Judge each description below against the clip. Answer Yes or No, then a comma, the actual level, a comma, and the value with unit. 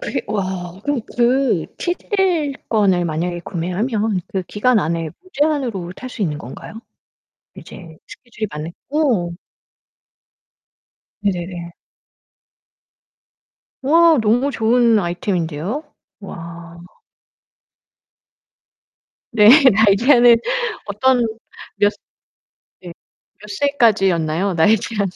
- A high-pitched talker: Yes, high, 205 Hz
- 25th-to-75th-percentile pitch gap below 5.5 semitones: No, wide, 6.0 semitones